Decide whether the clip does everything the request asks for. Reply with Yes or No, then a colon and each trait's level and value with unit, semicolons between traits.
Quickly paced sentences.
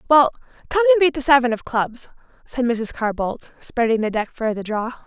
Yes: fast, 215 wpm